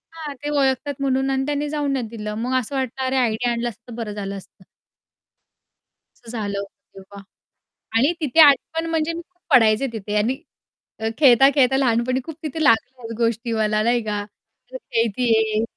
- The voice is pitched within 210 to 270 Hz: Yes, high, 245 Hz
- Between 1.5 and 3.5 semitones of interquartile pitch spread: No, average, 3.9 semitones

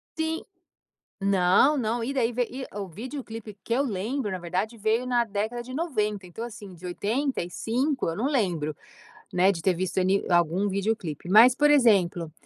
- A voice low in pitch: No, high, 215 Hz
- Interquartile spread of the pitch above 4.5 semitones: Yes, average, 5.1 semitones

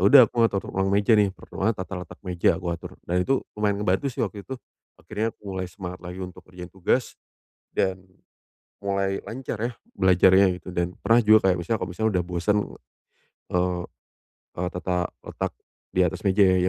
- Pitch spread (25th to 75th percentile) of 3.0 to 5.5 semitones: No, narrow, 2.5 semitones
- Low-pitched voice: Yes, very low, 95 Hz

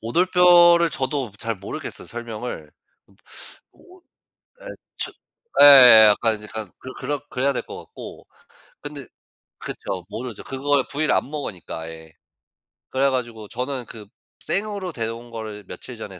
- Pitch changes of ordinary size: Yes, average, 4.8 semitones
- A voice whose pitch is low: Yes, low, 125 Hz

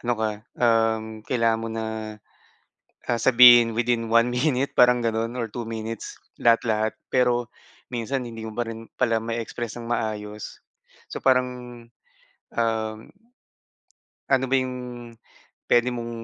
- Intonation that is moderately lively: No, narrow, 1.6 semitones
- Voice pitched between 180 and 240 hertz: No, low, 115 Hz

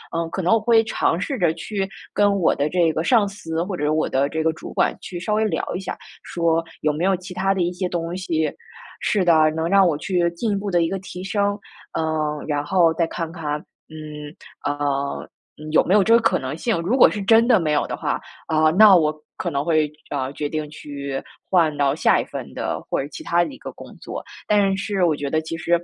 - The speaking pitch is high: No, medium, 170 Hz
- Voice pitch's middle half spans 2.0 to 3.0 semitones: No, average, 3.9 semitones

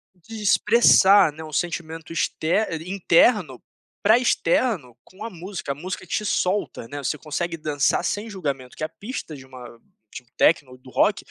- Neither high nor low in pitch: Yes, medium, 165 Hz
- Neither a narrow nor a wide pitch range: No, wide, 5.8 semitones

